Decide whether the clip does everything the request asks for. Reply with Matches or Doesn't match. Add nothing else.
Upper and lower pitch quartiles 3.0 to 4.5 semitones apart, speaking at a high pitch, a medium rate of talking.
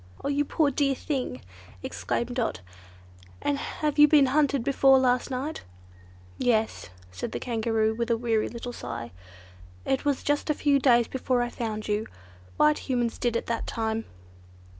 Matches